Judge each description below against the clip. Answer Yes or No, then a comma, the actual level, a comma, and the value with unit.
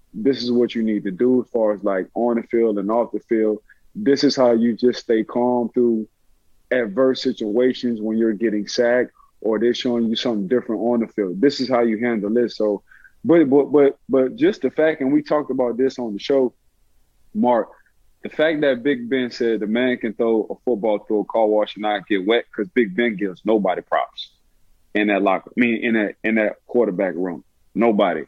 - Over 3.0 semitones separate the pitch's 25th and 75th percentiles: No, average, 2.7 semitones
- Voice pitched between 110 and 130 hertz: Yes, low, 120 Hz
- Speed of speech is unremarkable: No, fast, 215 wpm